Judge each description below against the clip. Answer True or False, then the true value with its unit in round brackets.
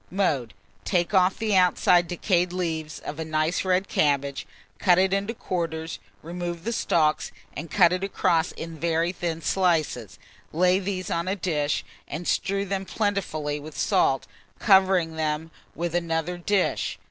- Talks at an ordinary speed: True (150 wpm)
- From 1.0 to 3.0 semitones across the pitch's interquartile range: True (2.7 semitones)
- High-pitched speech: False (175 Hz)